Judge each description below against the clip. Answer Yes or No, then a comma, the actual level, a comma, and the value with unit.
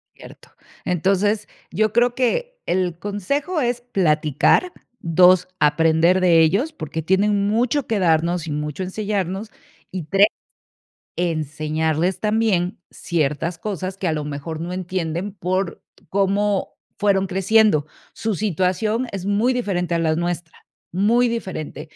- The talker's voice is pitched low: No, medium, 185 Hz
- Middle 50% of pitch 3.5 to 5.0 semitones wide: Yes, average, 4.1 semitones